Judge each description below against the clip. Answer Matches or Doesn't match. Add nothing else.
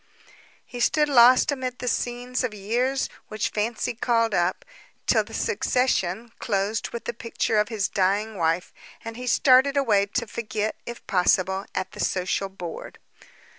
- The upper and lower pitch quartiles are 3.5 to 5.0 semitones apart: Matches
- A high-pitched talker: Matches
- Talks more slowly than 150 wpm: Doesn't match